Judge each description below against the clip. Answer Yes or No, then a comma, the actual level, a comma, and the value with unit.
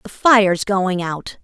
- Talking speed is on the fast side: No, average, 165 wpm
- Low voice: No, high, 195 Hz